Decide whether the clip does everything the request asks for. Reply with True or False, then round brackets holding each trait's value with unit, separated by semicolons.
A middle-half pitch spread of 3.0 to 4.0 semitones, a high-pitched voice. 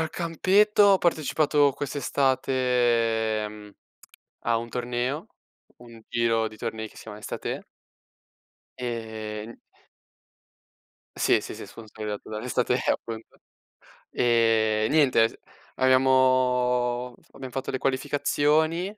False (3.3 semitones; 125 Hz)